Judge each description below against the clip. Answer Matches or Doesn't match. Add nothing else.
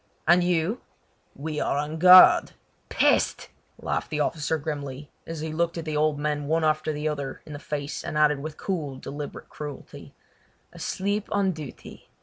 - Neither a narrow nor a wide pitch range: Doesn't match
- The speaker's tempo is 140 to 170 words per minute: Matches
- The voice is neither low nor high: Matches